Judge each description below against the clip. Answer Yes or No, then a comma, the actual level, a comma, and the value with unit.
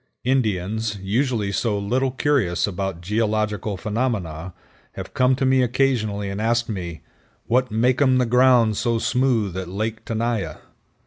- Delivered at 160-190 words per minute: No, slow, 135 wpm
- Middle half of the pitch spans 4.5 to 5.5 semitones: No, average, 3.9 semitones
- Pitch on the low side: Yes, low, 110 Hz